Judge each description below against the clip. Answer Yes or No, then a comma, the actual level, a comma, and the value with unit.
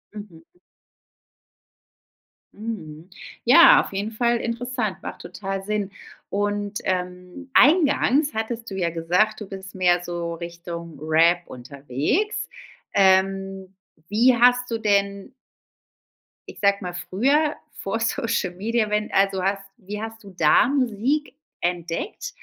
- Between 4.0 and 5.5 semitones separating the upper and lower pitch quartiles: Yes, average, 4.3 semitones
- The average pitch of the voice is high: Yes, high, 200 Hz